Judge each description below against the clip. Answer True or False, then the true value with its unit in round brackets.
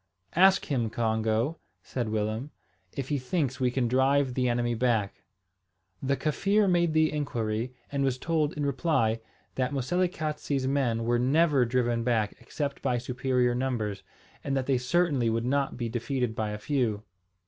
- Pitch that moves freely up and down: False (3.4 semitones)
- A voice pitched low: True (130 Hz)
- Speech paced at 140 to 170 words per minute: True (160 wpm)